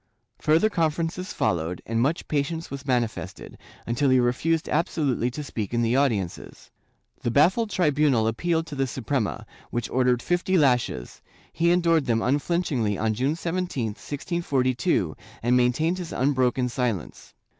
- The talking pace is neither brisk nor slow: Yes, average, 145 wpm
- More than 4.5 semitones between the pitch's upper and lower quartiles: Yes, wide, 5.5 semitones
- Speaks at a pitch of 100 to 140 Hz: Yes, low, 135 Hz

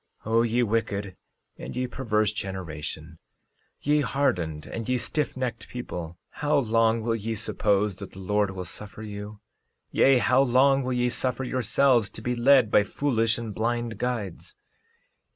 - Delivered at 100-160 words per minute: Yes, average, 155 wpm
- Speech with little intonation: No, average, 3.7 semitones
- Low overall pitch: Yes, low, 115 Hz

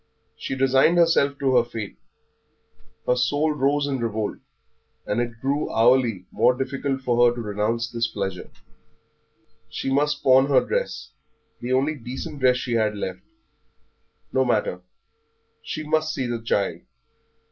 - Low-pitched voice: Yes, low, 130 Hz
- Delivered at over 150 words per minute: No, average, 145 wpm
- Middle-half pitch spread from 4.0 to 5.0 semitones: No, average, 3.3 semitones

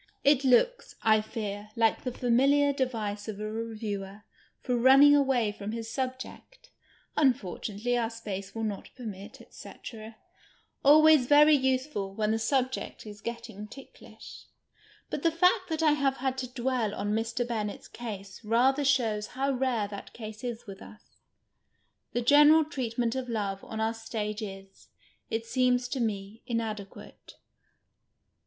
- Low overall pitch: No, high, 235 Hz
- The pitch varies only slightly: No, average, 3.8 semitones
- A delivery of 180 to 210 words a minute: No, average, 155 wpm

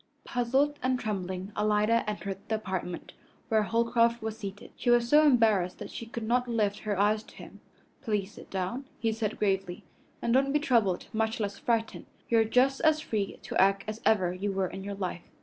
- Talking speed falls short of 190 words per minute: No, average, 200 wpm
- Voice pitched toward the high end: Yes, high, 220 Hz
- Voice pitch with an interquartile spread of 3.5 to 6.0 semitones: No, average, 3.1 semitones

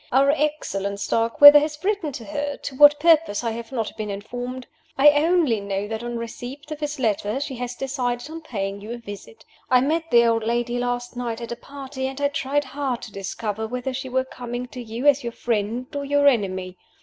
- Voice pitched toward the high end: Yes, very high, 250 Hz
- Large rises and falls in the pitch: No, average, 3.9 semitones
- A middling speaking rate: No, fast, 210 wpm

